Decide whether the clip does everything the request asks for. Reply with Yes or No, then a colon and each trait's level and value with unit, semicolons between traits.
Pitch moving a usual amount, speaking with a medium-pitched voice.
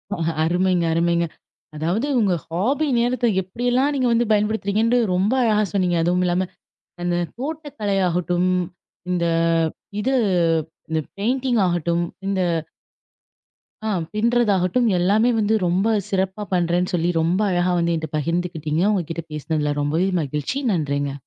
Yes: average, 4.4 semitones; medium, 180 Hz